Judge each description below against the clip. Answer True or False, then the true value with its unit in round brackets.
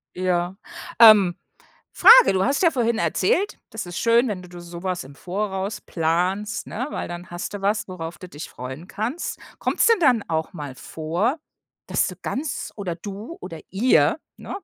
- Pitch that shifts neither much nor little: True (4.6 semitones)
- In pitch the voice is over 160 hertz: True (190 Hz)